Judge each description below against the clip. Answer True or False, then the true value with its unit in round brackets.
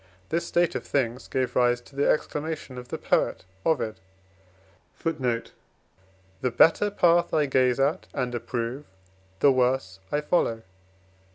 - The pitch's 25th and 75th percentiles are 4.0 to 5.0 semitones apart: True (4.4 semitones)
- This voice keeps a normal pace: False (125 wpm)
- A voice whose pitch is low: True (130 Hz)